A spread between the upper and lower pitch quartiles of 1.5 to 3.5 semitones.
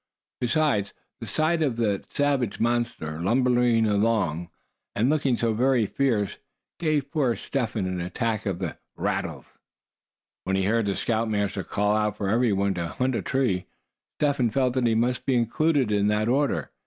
No: average, 4.1 semitones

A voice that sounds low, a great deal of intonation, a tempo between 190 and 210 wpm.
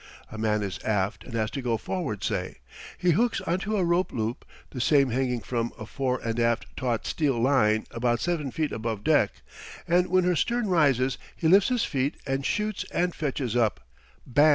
Yes: low, 130 Hz; wide, 6.8 semitones; average, 195 wpm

